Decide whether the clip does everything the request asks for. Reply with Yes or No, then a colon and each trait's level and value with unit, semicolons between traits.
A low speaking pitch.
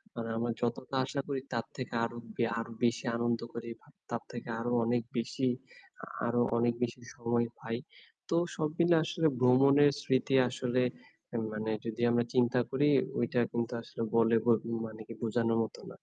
Yes: low, 120 Hz